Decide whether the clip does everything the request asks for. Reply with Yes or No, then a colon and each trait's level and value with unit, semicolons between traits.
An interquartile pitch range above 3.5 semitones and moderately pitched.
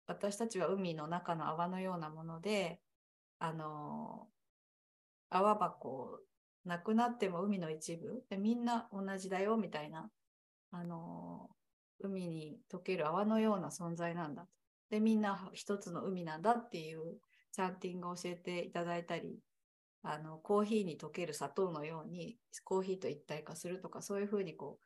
Yes: average, 4.1 semitones; medium, 180 Hz